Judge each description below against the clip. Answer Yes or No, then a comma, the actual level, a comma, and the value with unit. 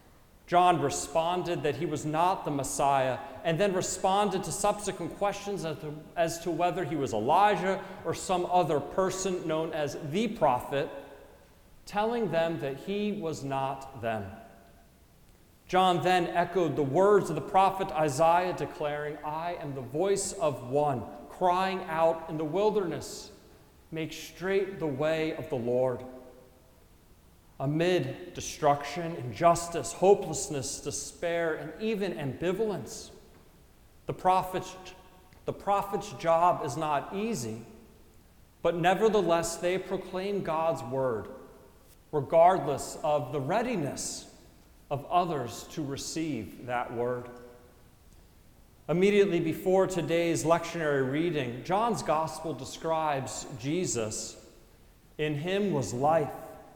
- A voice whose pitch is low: No, medium, 160 Hz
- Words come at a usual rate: No, slow, 115 wpm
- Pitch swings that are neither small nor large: Yes, average, 4.7 semitones